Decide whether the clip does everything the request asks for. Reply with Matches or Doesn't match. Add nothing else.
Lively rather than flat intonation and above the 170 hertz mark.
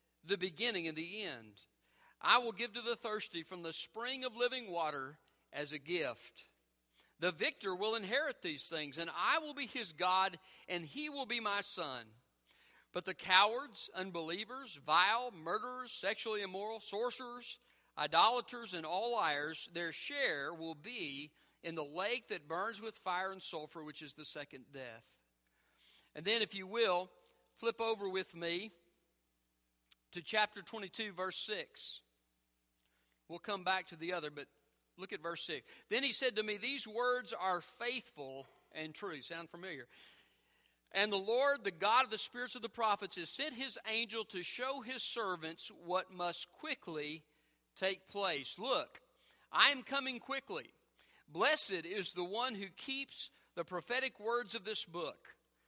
Matches